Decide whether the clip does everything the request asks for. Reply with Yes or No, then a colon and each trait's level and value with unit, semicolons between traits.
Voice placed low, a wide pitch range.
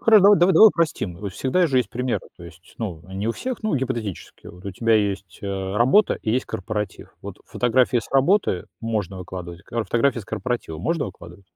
Yes: low, 115 Hz; wide, 5.8 semitones